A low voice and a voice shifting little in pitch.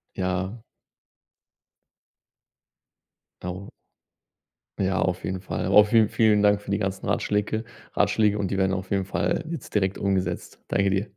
Yes: low, 100 Hz; narrow, 1.6 semitones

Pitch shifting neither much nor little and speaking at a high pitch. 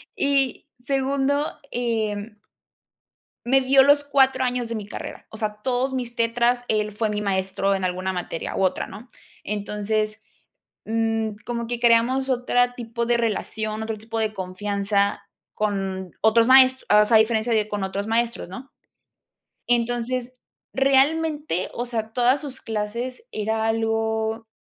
Yes: average, 3.0 semitones; high, 225 Hz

